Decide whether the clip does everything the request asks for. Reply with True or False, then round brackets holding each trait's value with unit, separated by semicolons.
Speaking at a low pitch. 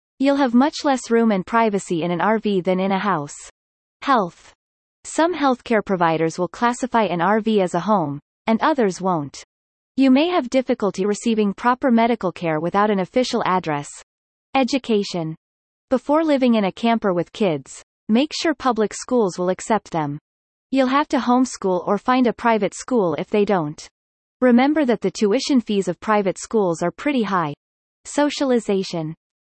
False (215 Hz)